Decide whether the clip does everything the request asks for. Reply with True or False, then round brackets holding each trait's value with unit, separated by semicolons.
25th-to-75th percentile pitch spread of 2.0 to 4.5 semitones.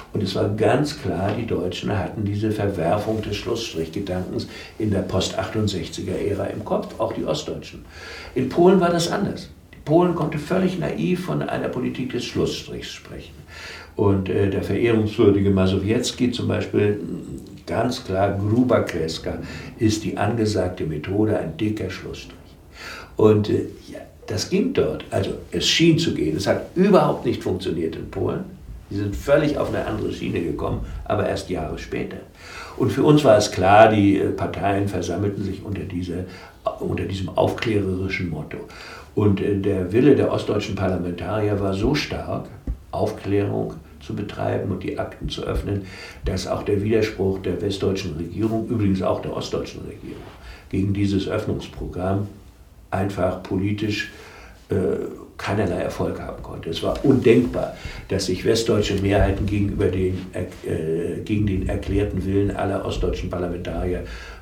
True (2.8 semitones)